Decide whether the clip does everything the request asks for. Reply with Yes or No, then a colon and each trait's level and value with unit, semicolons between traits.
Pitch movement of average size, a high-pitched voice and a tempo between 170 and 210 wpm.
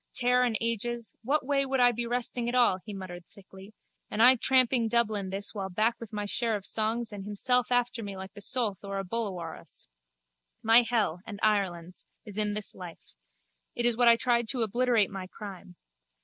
Yes: average, 3.4 semitones; high, 220 Hz; fast, 205 wpm